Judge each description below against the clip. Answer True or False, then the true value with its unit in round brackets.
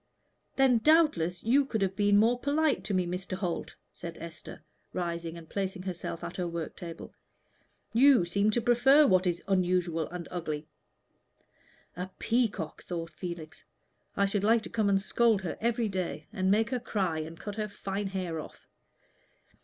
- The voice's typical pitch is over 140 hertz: True (190 Hz)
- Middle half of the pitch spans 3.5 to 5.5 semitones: True (4.6 semitones)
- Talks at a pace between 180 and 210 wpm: False (170 wpm)